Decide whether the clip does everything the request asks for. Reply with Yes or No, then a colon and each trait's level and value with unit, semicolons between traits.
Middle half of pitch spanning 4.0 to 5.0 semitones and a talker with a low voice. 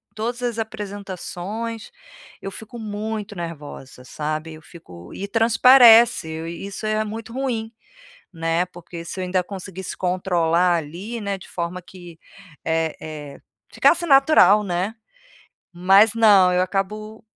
No: average, 4.4 semitones; high, 190 Hz